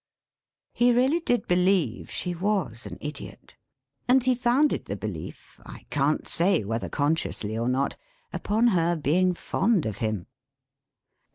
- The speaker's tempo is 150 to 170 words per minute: No, average, 140 wpm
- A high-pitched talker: No, medium, 175 Hz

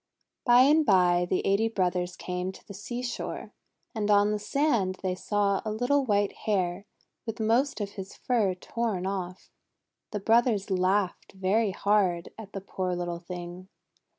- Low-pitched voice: No, high, 200 Hz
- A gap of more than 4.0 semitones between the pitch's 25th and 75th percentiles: No, average, 3.2 semitones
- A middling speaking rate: Yes, average, 155 wpm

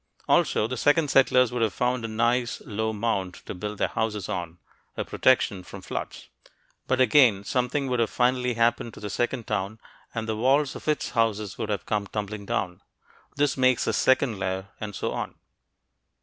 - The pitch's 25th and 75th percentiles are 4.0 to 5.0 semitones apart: No, average, 3.5 semitones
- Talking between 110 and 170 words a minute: No, average, 185 wpm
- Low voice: Yes, low, 115 Hz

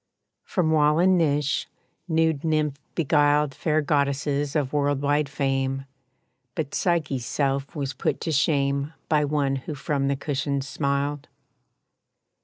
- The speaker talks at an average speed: No, slow, 130 wpm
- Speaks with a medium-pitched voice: Yes, medium, 145 Hz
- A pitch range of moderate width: No, narrow, 1.7 semitones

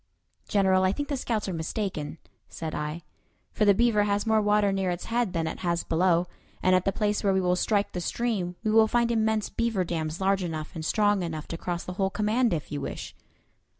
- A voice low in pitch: No, high, 195 Hz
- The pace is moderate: No, fast, 220 wpm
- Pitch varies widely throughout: No, average, 3.7 semitones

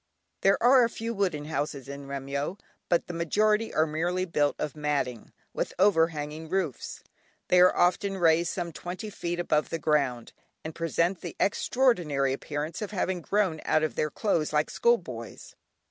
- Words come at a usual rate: Yes, average, 170 wpm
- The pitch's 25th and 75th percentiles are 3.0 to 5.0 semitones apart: Yes, average, 4.1 semitones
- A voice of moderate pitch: Yes, medium, 165 Hz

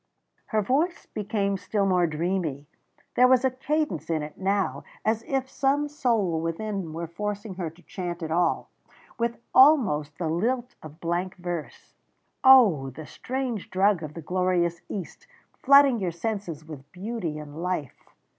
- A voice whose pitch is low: No, medium, 185 Hz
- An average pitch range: No, wide, 6.0 semitones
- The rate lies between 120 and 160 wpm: Yes, average, 155 wpm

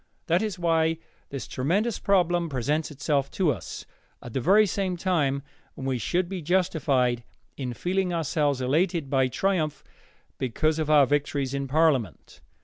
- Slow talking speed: No, average, 145 wpm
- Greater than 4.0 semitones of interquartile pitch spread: Yes, average, 4.6 semitones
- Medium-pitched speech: Yes, medium, 155 Hz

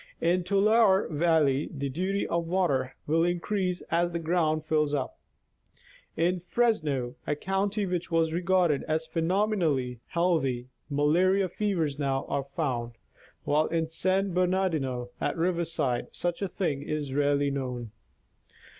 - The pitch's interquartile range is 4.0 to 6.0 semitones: Yes, average, 4.3 semitones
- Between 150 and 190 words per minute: No, slow, 135 wpm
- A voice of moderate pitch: Yes, medium, 165 Hz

